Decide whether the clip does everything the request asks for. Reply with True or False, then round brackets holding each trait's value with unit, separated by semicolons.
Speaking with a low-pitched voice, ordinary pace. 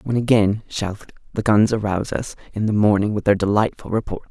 True (105 Hz; 195 wpm)